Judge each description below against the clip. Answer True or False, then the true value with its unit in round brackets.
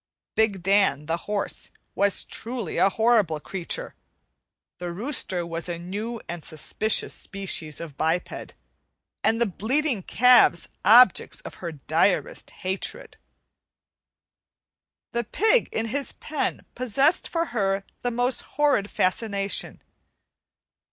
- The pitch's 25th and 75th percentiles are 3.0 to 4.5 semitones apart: False (5.5 semitones)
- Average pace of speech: False (115 wpm)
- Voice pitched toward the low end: False (205 Hz)